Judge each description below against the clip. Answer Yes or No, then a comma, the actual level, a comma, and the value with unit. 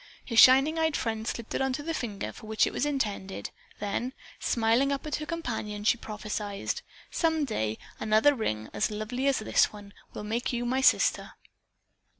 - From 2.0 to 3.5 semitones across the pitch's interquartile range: No, average, 4.5 semitones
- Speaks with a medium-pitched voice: No, high, 235 Hz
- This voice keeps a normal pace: Yes, average, 175 wpm